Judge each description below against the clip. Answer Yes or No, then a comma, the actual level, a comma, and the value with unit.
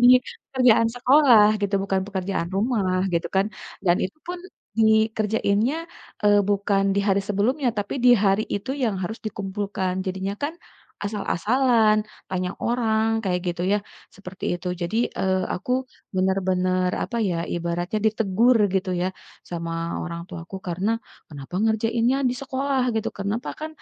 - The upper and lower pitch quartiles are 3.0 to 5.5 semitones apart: Yes, average, 3.6 semitones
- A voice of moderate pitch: No, high, 205 Hz